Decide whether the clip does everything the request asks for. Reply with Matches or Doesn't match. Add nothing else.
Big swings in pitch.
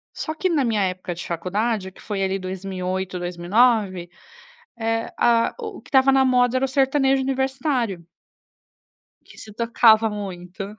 Matches